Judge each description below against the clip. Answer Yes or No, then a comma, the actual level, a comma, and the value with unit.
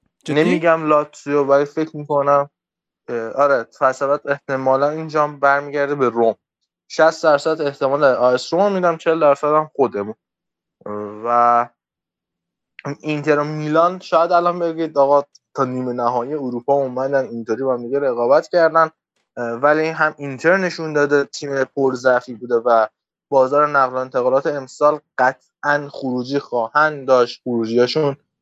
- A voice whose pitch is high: No, medium, 140 Hz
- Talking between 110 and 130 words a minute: Yes, average, 120 wpm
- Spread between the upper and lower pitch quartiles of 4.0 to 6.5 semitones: No, average, 3.2 semitones